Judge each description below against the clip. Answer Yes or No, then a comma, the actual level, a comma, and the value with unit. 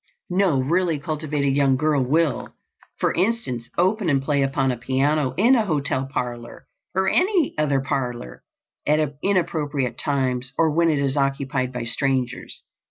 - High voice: No, medium, 140 Hz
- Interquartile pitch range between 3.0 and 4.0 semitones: Yes, average, 3.7 semitones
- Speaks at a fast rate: No, average, 150 wpm